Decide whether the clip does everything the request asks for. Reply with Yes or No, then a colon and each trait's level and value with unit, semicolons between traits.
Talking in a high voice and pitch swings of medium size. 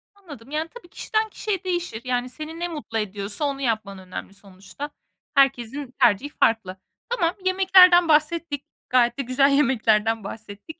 No: very high, 275 Hz; wide, 6.9 semitones